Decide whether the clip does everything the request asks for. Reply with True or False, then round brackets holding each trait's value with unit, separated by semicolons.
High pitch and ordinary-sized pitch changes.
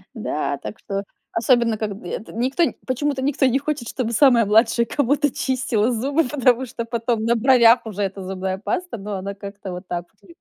True (230 Hz; 4.3 semitones)